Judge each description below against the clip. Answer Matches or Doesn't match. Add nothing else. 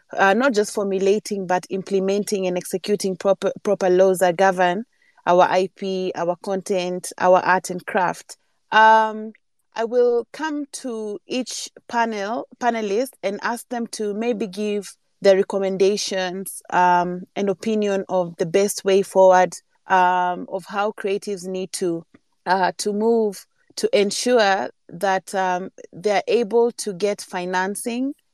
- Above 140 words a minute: Doesn't match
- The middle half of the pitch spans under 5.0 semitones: Matches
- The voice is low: Doesn't match